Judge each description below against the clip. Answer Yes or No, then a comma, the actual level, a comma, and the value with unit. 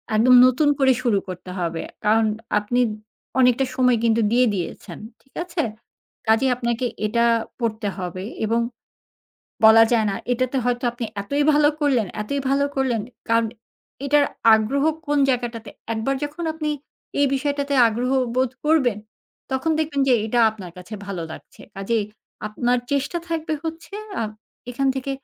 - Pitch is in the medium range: No, high, 245 Hz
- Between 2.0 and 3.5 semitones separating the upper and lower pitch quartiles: No, average, 4.1 semitones